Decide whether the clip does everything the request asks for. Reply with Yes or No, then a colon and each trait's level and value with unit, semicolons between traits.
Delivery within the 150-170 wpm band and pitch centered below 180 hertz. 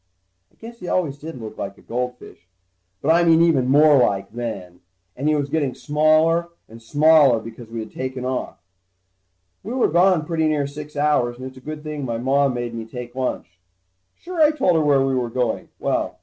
No: fast, 205 wpm; medium, 140 Hz